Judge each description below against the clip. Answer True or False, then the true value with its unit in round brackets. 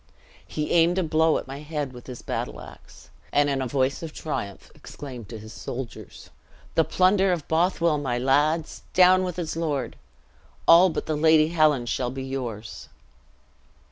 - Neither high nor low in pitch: True (150 Hz)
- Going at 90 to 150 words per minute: False (170 wpm)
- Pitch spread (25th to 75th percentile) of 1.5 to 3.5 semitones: False (4.1 semitones)